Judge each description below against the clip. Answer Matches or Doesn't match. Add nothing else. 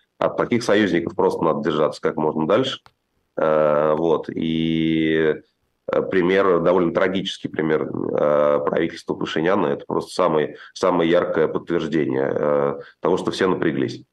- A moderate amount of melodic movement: Doesn't match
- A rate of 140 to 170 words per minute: Doesn't match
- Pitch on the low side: Matches